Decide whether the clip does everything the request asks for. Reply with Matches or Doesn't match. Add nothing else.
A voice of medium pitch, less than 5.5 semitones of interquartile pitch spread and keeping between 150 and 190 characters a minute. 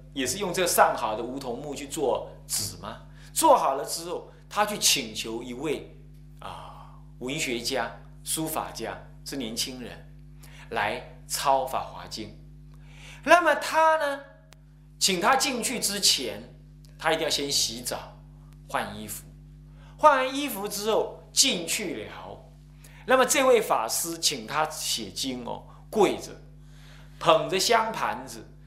Matches